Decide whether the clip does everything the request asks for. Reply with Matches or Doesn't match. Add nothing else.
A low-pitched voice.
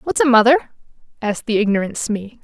Doesn't match